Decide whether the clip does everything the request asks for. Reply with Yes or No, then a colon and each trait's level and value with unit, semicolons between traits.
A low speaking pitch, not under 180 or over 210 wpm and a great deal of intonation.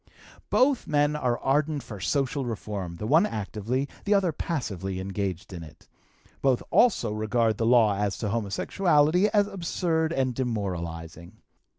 No: low, 120 Hz; average, 145 wpm; wide, 7.2 semitones